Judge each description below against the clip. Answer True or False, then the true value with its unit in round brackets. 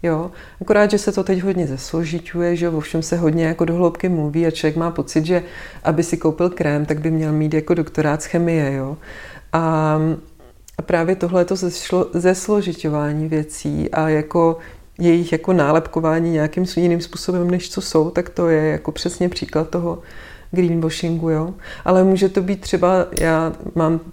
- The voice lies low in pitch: False (165 Hz)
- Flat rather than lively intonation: True (2.1 semitones)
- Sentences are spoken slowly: False (170 wpm)